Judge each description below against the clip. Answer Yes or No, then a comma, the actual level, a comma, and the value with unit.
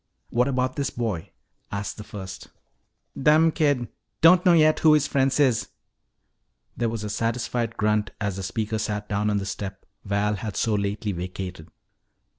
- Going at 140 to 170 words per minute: Yes, average, 165 wpm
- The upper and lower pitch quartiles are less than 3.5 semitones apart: No, average, 4.2 semitones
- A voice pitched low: Yes, low, 110 Hz